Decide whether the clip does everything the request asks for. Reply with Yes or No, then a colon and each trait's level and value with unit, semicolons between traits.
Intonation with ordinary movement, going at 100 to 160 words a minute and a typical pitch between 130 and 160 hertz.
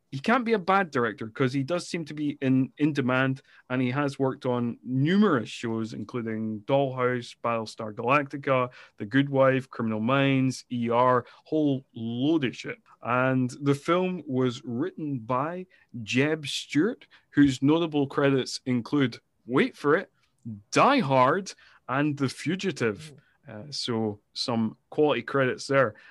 Yes: average, 3.0 semitones; average, 140 wpm; low, 135 Hz